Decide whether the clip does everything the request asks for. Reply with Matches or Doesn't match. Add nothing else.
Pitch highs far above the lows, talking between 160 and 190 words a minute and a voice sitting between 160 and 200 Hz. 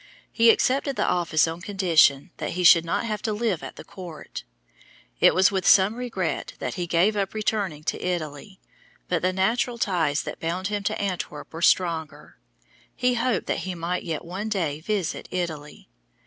Doesn't match